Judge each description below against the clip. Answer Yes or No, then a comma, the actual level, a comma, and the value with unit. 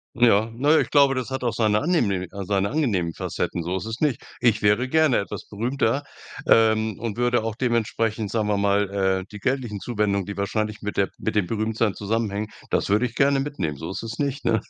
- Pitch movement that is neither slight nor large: Yes, average, 3.4 semitones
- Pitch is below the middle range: Yes, low, 110 Hz